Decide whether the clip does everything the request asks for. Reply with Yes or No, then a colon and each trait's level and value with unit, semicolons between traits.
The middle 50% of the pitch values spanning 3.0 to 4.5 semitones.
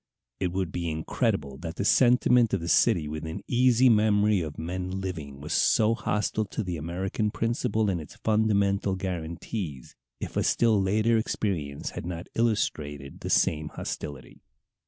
No: average, 5.3 semitones